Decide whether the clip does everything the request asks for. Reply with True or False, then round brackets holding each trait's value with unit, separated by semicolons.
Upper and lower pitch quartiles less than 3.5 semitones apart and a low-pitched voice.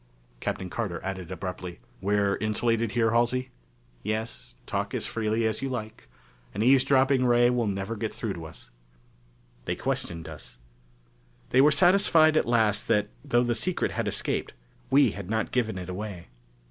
False (3.8 semitones; 110 Hz)